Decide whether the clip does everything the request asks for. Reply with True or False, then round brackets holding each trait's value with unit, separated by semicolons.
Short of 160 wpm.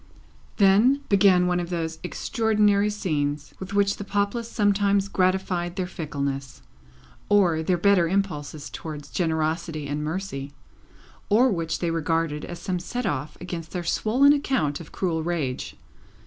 True (140 wpm)